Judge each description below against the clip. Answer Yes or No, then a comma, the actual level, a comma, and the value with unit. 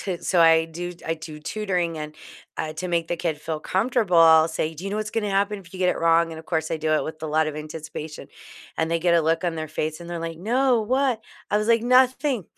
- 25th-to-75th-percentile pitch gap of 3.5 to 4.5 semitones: Yes, average, 4.2 semitones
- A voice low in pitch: No, medium, 170 Hz